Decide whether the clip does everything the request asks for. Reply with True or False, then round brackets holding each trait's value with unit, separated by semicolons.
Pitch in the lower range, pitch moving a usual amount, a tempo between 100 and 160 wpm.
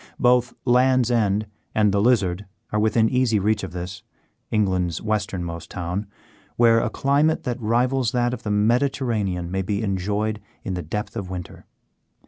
True (105 Hz; 4.2 semitones; 155 wpm)